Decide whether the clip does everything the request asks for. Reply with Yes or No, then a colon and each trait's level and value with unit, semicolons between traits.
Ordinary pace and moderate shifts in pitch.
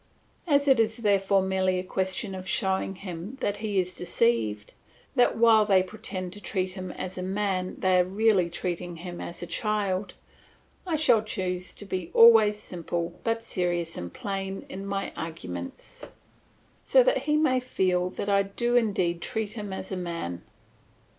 Yes: average, 170 wpm; average, 3.0 semitones